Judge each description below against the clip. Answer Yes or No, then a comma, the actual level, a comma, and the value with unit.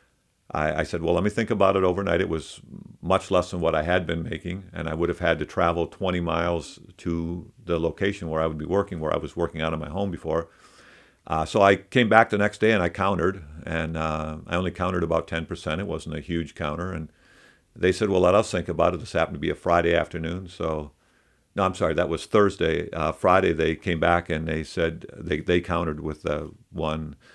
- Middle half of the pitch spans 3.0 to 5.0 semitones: No, narrow, 2.5 semitones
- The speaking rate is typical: No, fast, 230 wpm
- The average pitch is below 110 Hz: Yes, very low, 85 Hz